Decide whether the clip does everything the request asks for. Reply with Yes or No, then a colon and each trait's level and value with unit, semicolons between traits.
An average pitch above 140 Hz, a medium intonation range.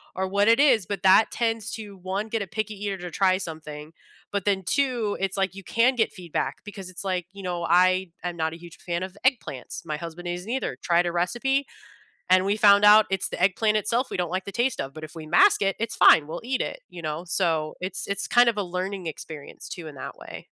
Yes: high, 190 Hz; average, 3.5 semitones